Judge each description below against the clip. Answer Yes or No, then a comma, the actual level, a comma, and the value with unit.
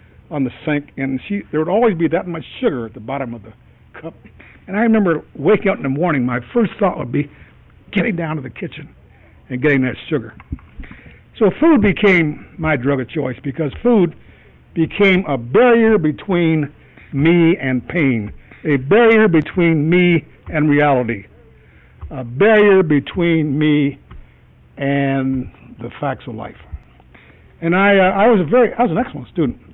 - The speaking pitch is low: No, medium, 150 Hz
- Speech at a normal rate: Yes, average, 165 wpm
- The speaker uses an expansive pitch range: Yes, wide, 6.0 semitones